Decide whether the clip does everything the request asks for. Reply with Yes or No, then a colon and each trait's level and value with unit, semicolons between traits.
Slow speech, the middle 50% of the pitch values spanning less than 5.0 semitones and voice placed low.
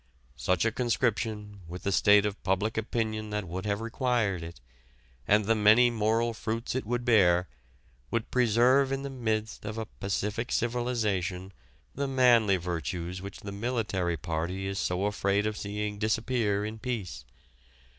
No: average, 155 wpm; average, 3.2 semitones; low, 105 Hz